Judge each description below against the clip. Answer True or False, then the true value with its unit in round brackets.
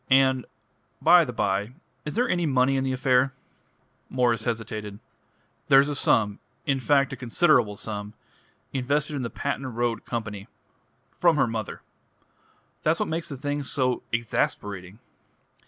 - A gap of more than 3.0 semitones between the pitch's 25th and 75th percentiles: True (3.8 semitones)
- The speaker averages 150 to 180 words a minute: False (140 wpm)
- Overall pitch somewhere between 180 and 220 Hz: False (130 Hz)